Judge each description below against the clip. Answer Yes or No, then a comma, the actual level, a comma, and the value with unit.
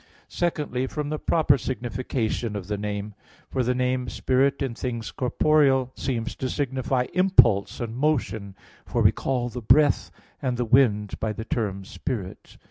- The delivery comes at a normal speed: Yes, average, 155 wpm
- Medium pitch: No, low, 125 Hz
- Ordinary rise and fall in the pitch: Yes, average, 3.4 semitones